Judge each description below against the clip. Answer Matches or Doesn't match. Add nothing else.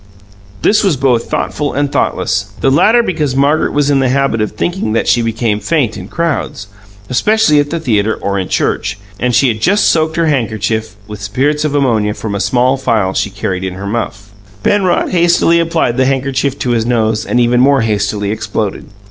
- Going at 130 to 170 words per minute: Doesn't match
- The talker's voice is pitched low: Matches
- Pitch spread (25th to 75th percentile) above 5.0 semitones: Matches